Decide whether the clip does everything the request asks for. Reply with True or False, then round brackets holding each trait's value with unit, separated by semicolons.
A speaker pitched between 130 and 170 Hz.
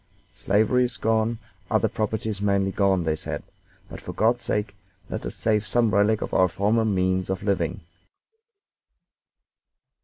False (105 Hz)